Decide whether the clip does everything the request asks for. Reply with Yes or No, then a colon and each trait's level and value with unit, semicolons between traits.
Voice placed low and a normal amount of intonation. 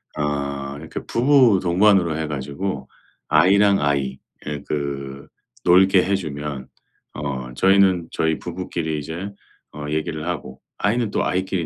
Yes: very low, 80 Hz; average, 4.9 semitones